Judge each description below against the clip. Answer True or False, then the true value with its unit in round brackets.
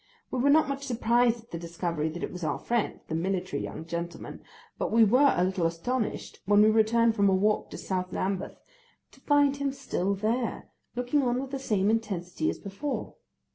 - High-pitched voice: True (215 Hz)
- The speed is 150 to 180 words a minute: False (200 wpm)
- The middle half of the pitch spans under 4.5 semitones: False (5.4 semitones)